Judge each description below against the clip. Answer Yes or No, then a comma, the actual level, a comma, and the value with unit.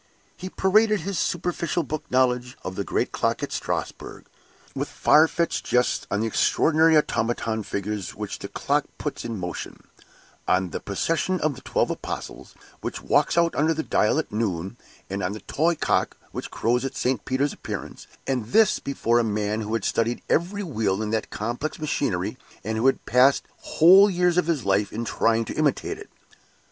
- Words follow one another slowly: No, average, 180 wpm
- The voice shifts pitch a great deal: Yes, wide, 7.0 semitones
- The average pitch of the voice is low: Yes, low, 125 Hz